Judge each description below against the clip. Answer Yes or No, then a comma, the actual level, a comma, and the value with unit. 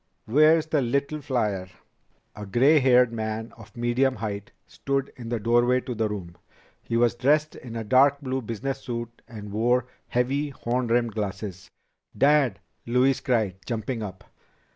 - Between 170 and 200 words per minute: No, average, 155 wpm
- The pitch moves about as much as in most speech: Yes, average, 3.4 semitones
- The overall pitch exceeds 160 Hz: No, low, 120 Hz